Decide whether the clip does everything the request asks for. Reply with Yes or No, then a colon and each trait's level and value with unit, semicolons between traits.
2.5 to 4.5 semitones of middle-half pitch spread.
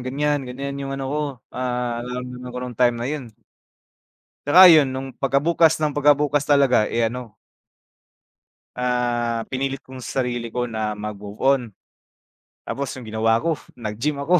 Yes: average, 2.8 semitones